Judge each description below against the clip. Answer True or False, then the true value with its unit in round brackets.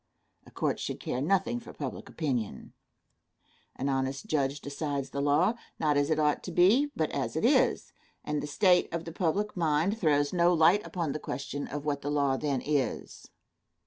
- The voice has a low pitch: False (150 Hz)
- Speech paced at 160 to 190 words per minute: True (185 wpm)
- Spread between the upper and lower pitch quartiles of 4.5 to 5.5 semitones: False (3.8 semitones)